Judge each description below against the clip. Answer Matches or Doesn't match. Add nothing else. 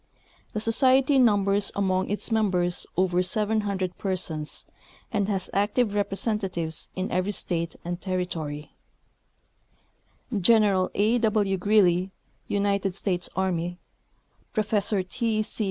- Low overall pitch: Doesn't match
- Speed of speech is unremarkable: Doesn't match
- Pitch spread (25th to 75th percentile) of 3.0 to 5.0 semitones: Doesn't match